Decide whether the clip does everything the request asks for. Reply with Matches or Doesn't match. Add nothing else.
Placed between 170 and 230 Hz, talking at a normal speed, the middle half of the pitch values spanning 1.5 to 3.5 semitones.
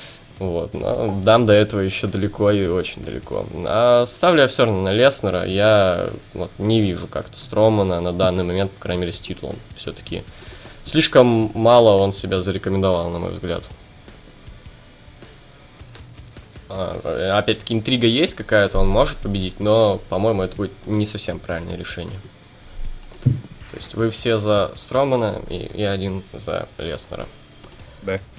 Doesn't match